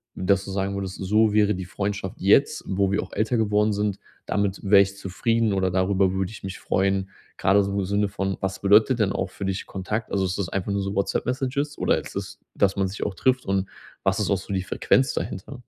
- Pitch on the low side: Yes, low, 100 Hz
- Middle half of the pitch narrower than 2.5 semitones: Yes, narrow, 1.6 semitones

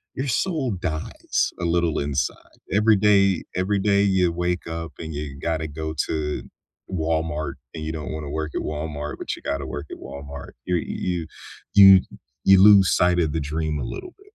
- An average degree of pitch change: Yes, average, 3.8 semitones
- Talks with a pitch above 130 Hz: No, very low, 80 Hz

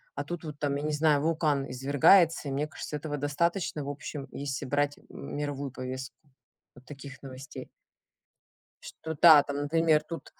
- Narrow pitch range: Yes, narrow, 2.0 semitones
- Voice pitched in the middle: Yes, medium, 145 Hz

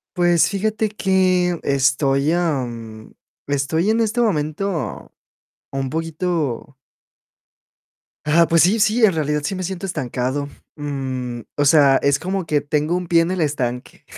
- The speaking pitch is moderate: Yes, medium, 155 Hz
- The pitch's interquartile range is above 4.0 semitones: Yes, average, 4.8 semitones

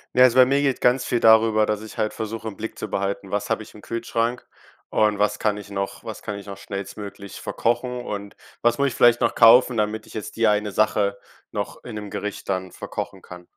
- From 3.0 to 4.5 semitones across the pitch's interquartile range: No, narrow, 2.4 semitones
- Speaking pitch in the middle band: No, low, 110 Hz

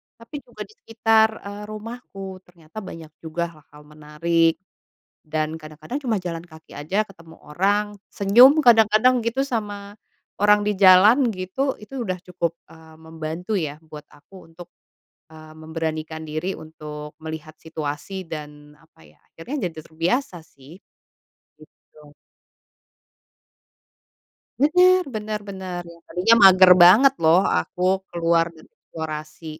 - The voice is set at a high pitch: No, medium, 175 Hz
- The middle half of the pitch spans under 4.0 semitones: No, average, 4.9 semitones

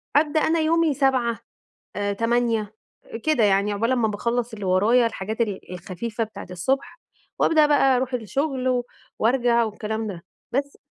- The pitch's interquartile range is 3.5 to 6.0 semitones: Yes, average, 4.2 semitones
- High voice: Yes, high, 235 Hz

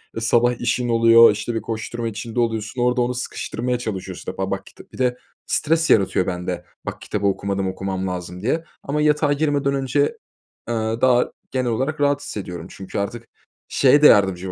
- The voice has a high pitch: No, low, 115 Hz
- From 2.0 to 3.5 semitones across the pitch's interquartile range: No, average, 4.7 semitones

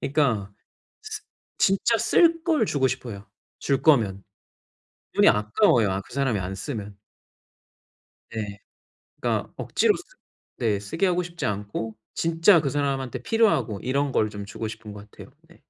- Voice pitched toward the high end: No, low, 125 Hz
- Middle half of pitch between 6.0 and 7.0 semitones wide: No, wide, 7.8 semitones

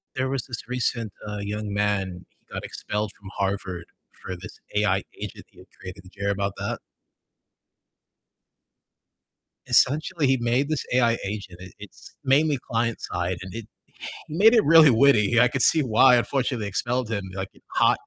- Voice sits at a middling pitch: No, low, 110 Hz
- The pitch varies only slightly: No, average, 4.7 semitones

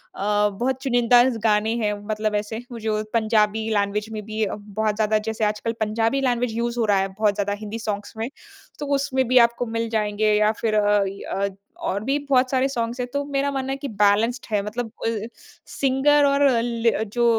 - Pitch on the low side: No, high, 225 Hz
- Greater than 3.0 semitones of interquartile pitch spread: No, average, 2.7 semitones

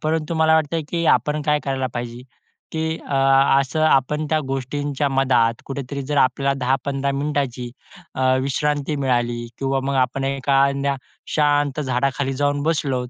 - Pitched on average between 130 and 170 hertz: Yes, medium, 140 Hz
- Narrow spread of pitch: Yes, narrow, 2.0 semitones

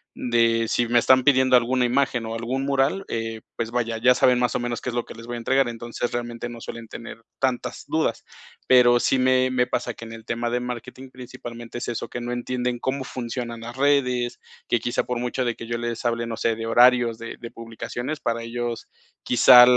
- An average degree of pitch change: No, narrow, 1.4 semitones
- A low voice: Yes, low, 120 Hz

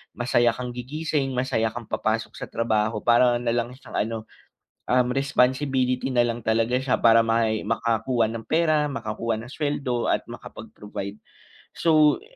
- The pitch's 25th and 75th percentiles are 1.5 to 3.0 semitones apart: Yes, narrow, 2.4 semitones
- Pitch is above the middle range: No, low, 120 Hz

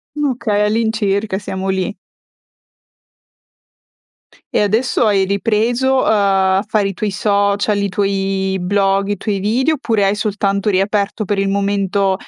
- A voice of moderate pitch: No, high, 200 Hz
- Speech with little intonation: Yes, narrow, 1.5 semitones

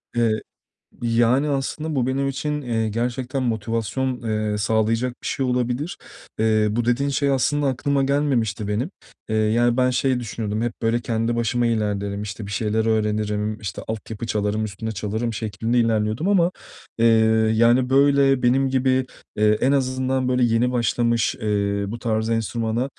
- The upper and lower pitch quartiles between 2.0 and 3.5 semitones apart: Yes, average, 3.1 semitones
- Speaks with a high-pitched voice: No, low, 115 Hz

